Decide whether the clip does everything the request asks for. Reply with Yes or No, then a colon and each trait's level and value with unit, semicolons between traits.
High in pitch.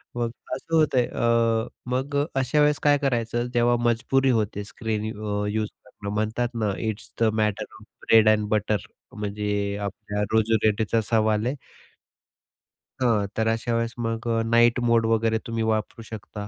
No: low, 115 Hz